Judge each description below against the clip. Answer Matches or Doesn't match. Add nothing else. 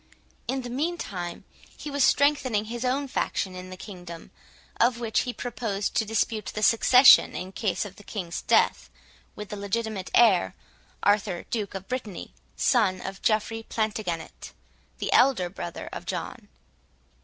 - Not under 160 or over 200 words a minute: Doesn't match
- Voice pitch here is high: Matches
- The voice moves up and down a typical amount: Matches